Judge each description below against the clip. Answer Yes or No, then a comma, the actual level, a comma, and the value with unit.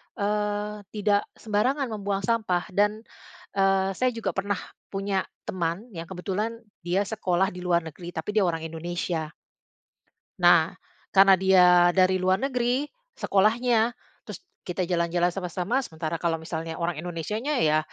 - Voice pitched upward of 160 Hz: Yes, high, 190 Hz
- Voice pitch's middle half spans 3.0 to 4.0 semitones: Yes, average, 3.3 semitones